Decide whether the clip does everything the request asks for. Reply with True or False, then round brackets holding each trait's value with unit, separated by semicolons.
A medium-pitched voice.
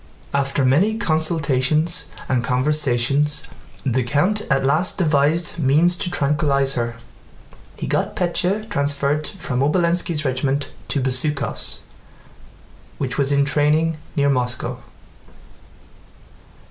True (145 Hz)